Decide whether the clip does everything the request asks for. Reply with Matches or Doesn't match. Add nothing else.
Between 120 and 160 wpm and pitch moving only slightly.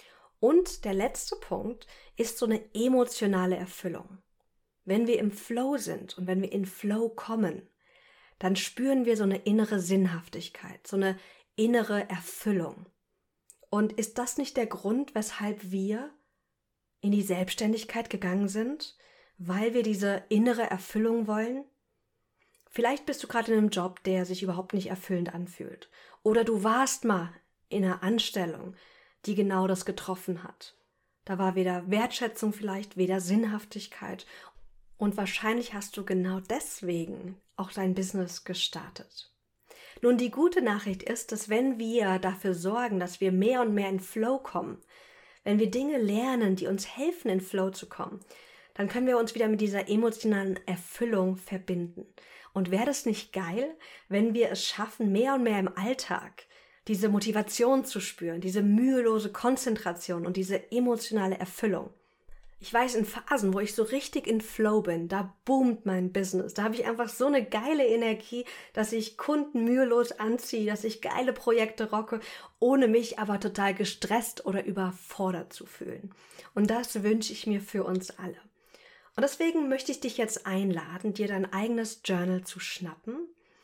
Doesn't match